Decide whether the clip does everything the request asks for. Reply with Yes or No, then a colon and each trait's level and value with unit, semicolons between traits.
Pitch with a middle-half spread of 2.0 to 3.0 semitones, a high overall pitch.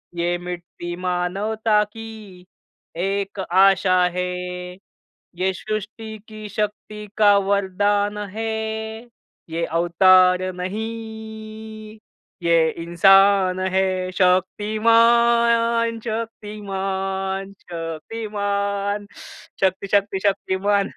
Yes: narrow, 2.6 semitones; high, 200 Hz